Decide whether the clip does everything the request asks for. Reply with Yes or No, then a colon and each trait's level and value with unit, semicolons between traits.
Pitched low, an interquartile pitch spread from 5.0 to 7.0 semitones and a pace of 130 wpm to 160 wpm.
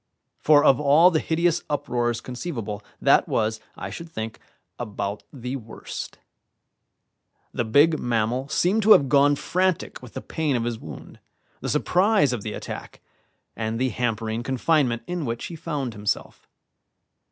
Yes: low, 130 Hz; wide, 5.6 semitones; average, 150 wpm